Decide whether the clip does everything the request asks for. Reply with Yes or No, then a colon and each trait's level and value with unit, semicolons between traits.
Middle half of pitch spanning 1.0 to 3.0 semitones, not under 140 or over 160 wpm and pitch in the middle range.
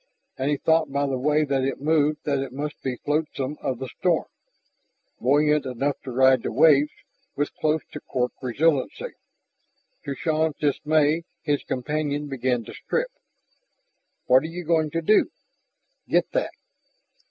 Yes: narrow, 2.6 semitones; average, 155 wpm; medium, 145 Hz